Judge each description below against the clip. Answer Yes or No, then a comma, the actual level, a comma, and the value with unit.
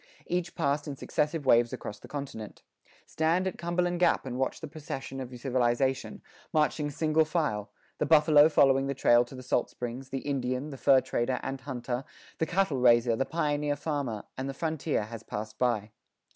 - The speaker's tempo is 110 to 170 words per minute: No, average, 180 wpm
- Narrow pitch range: No, average, 3.8 semitones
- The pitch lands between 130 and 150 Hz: Yes, low, 135 Hz